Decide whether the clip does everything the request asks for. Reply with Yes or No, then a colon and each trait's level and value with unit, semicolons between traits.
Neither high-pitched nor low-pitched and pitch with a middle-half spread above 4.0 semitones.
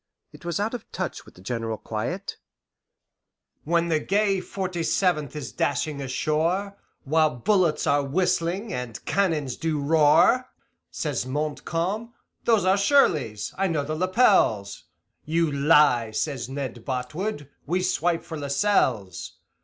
Yes: medium, 155 Hz; average, 5.2 semitones